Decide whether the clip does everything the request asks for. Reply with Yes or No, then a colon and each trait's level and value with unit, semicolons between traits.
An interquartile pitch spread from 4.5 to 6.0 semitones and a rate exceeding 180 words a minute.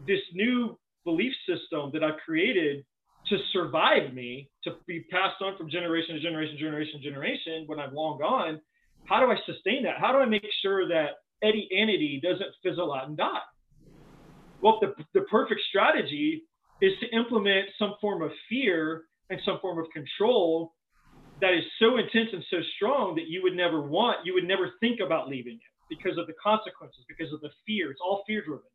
Yes: average, 5.2 semitones; average, 190 wpm